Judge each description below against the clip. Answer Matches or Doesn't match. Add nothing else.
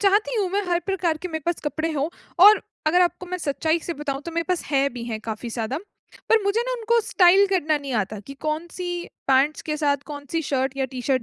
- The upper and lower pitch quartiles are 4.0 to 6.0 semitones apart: Matches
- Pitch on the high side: Matches